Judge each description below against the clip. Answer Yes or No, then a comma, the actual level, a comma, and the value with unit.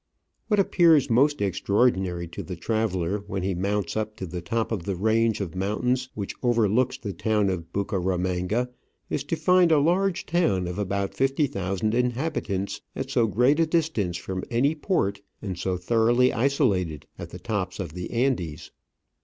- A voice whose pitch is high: No, low, 110 Hz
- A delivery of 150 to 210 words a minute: Yes, average, 170 wpm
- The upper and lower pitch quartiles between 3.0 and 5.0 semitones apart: No, wide, 5.6 semitones